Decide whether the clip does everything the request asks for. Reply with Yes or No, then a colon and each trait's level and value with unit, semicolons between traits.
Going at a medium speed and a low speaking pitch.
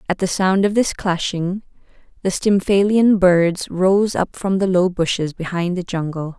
No: average, 170 wpm; medium, 185 Hz